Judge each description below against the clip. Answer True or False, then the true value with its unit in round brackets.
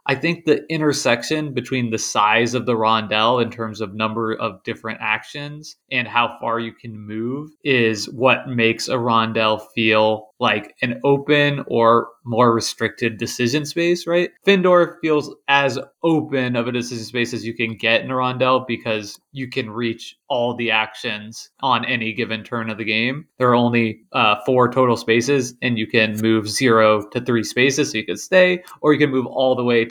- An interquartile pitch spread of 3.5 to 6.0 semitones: False (3.0 semitones)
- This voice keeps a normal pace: True (190 wpm)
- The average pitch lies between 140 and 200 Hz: False (120 Hz)